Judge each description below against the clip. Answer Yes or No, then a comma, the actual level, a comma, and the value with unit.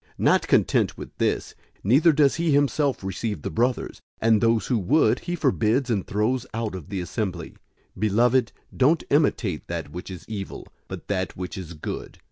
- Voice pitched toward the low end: Yes, low, 110 Hz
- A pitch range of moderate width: No, wide, 5.7 semitones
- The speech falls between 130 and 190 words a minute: Yes, average, 175 wpm